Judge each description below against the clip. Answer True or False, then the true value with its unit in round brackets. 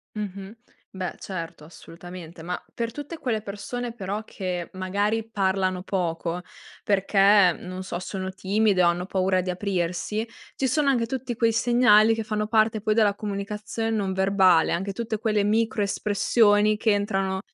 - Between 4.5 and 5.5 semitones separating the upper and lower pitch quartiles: False (2.8 semitones)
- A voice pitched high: True (200 Hz)